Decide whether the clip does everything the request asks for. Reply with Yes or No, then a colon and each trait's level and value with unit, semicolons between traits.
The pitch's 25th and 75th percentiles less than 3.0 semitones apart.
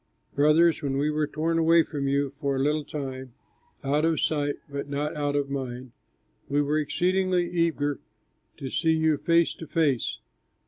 Yes: narrow, 2.4 semitones